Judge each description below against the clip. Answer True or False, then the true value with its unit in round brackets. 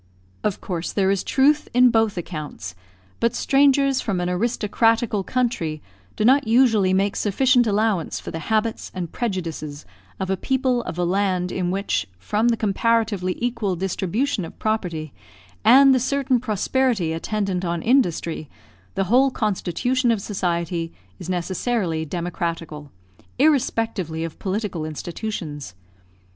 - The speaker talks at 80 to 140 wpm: True (135 wpm)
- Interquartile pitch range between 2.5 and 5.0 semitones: False (5.4 semitones)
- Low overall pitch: False (200 Hz)